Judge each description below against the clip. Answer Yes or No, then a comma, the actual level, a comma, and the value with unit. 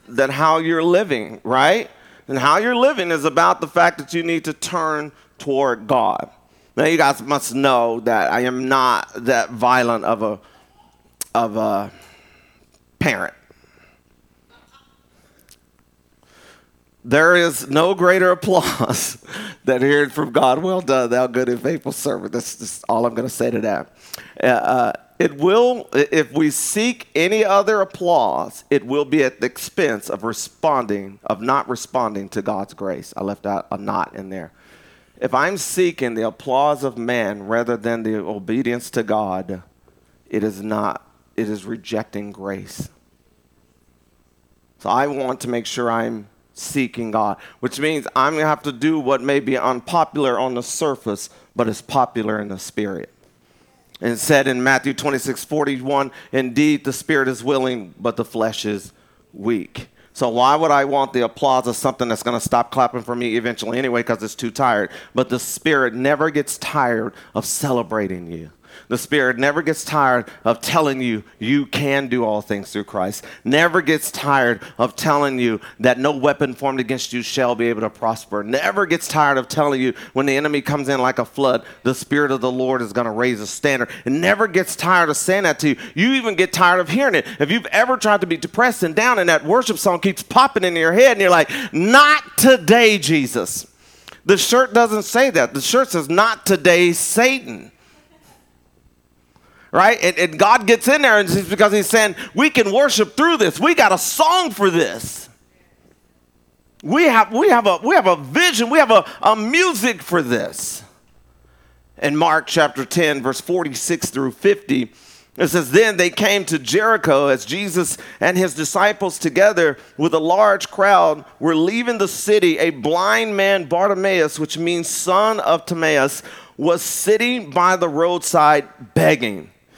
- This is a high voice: No, medium, 140 Hz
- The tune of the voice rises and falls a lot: Yes, wide, 7.4 semitones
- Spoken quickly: No, average, 175 wpm